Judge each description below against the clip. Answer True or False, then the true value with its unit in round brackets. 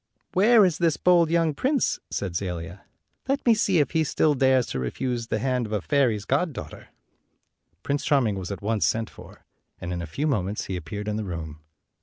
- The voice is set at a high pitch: False (120 Hz)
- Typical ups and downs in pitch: False (8.6 semitones)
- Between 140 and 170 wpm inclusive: False (200 wpm)